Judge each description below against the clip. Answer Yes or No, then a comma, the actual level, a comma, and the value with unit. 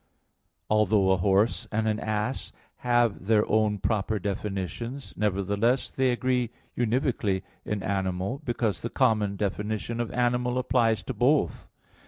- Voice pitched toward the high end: No, low, 110 Hz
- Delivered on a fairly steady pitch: No, average, 3.3 semitones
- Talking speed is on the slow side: Yes, slow, 130 wpm